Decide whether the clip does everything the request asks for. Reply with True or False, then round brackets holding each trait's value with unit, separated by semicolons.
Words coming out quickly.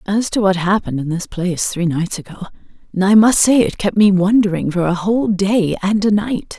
True (220 wpm)